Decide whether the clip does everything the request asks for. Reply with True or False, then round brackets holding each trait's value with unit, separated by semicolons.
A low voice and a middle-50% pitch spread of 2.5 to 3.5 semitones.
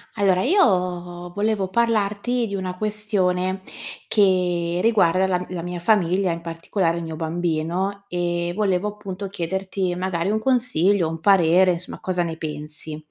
False (185 Hz; 2.8 semitones)